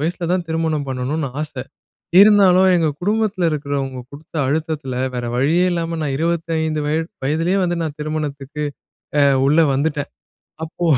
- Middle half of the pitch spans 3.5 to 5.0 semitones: No, average, 3.0 semitones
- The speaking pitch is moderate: Yes, medium, 155 Hz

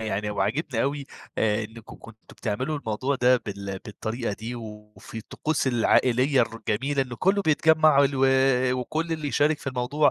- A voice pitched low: Yes, low, 125 Hz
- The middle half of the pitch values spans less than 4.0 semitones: No, average, 4.8 semitones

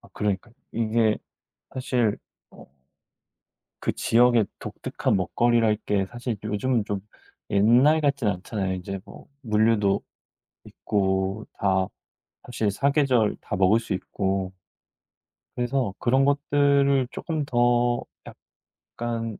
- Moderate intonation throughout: Yes, average, 3.7 semitones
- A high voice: No, low, 115 Hz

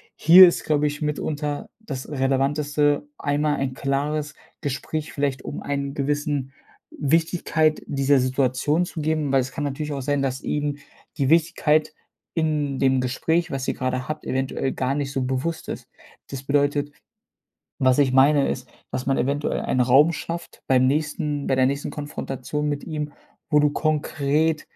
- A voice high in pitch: No, medium, 145 Hz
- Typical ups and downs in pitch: No, narrow, 2.0 semitones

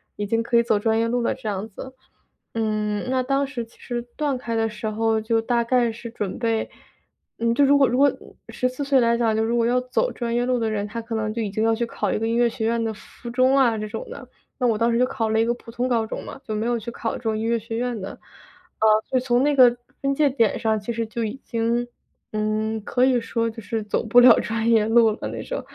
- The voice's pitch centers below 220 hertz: No, high, 230 Hz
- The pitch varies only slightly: Yes, narrow, 1.9 semitones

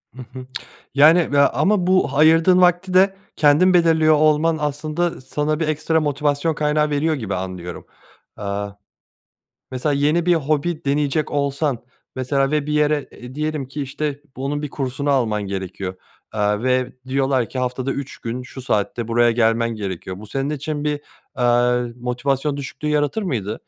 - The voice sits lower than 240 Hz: Yes, medium, 140 Hz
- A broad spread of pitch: No, average, 3.5 semitones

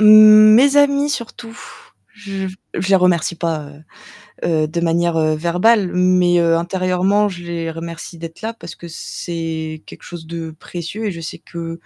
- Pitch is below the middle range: No, medium, 175 Hz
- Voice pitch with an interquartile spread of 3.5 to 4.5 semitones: No, average, 2.7 semitones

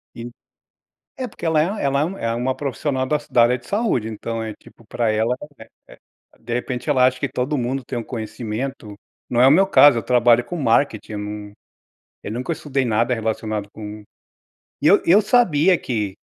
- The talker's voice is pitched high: No, low, 125 Hz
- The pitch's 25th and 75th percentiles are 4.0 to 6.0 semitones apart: Yes, average, 4.4 semitones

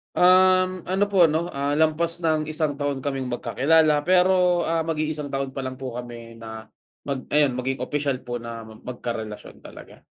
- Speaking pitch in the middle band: Yes, medium, 145 Hz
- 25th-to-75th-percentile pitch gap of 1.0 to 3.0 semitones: No, average, 4.5 semitones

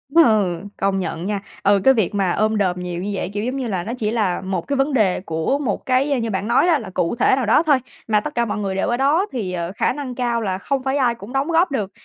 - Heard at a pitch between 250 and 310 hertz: No, high, 220 Hz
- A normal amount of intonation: No, wide, 5.7 semitones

